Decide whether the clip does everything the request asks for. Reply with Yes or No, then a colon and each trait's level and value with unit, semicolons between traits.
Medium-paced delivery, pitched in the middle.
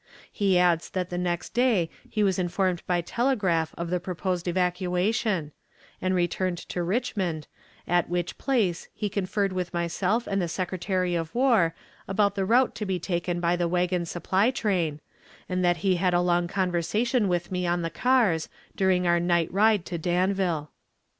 Yes: average, 170 wpm; medium, 180 Hz